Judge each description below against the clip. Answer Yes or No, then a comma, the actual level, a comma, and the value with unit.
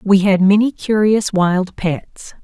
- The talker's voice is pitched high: Yes, high, 195 Hz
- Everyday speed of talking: Yes, average, 150 wpm